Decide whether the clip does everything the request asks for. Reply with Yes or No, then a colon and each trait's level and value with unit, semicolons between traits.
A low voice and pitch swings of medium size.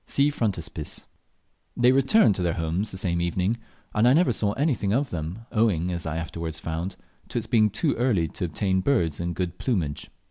No: very low, 95 Hz; wide, 5.9 semitones